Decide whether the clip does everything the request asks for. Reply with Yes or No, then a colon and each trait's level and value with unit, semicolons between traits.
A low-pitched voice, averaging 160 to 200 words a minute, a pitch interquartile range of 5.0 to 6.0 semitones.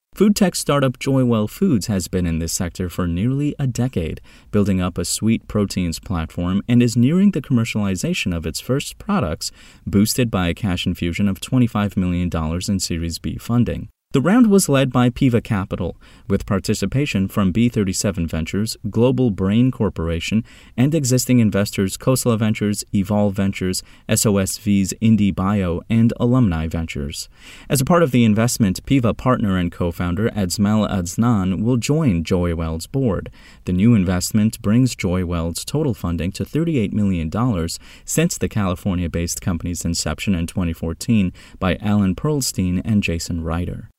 No: low, 100 Hz; average, 150 wpm; average, 5.3 semitones